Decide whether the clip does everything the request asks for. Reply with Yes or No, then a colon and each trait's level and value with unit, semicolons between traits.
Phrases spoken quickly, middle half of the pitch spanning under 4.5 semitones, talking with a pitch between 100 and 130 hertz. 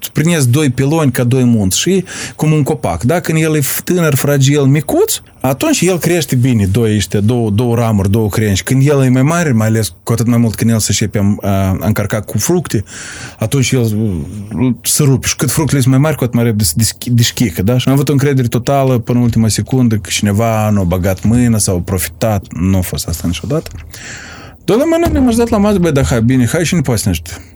No: fast, 230 wpm; average, 5.1 semitones; low, 120 Hz